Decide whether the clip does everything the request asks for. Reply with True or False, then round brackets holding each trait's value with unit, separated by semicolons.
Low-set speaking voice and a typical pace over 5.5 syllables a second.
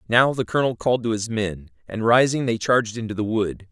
True (115 Hz; 6.0 syllables/s)